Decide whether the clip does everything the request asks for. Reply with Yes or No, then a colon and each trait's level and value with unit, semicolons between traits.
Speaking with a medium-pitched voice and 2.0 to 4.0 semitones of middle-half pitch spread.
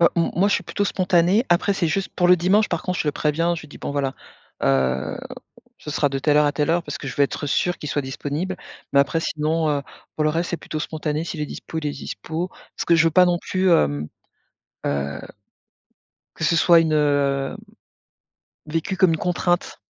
Yes: medium, 160 Hz; average, 3.3 semitones